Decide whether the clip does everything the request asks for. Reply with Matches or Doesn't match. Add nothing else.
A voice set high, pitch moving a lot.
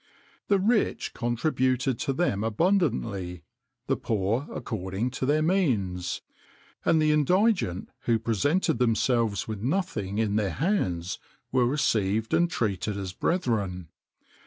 Doesn't match